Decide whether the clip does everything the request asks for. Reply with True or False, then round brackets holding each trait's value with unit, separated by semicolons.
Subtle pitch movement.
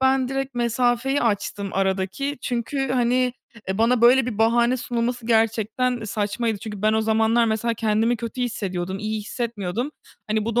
True (2.3 semitones)